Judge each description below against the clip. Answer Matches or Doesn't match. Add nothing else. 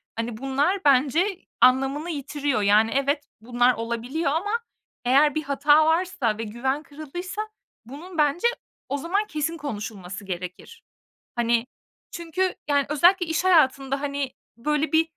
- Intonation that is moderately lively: Matches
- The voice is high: Matches